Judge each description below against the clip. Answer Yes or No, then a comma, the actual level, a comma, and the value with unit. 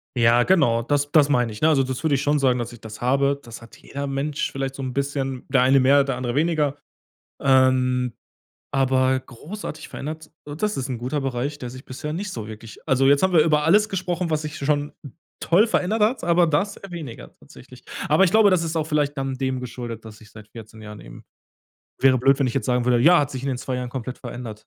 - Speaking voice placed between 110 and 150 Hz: Yes, low, 135 Hz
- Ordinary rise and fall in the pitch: Yes, average, 3.4 semitones